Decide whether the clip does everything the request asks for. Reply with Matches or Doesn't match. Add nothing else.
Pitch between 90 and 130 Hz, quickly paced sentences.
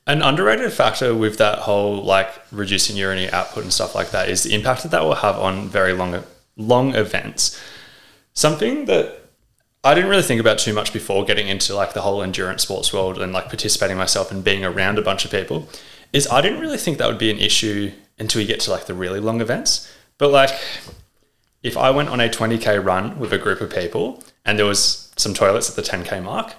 Matches